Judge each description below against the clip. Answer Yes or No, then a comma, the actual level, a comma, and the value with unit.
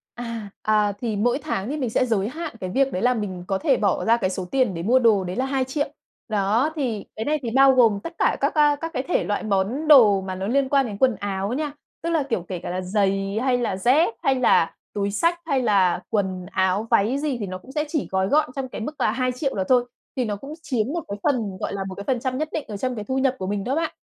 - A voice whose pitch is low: No, high, 230 Hz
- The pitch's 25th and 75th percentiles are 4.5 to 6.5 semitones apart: Yes, average, 5.2 semitones